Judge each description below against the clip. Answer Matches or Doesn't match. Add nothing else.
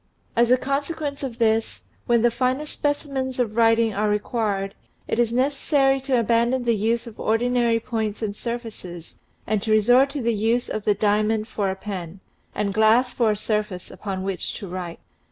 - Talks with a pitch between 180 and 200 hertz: Doesn't match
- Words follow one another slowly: Doesn't match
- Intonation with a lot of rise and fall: Doesn't match